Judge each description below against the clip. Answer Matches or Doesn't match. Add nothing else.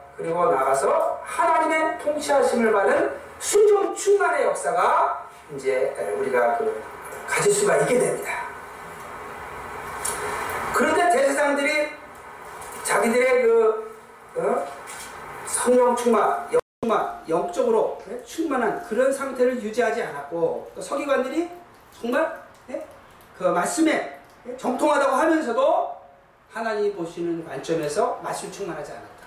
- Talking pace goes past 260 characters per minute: Doesn't match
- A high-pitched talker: Matches